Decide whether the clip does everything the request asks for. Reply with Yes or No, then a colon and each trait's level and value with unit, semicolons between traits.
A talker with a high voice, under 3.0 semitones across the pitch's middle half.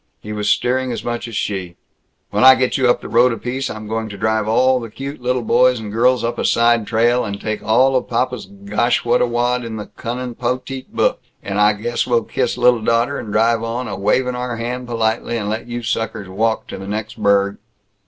No: low, 115 Hz; narrow, 2.4 semitones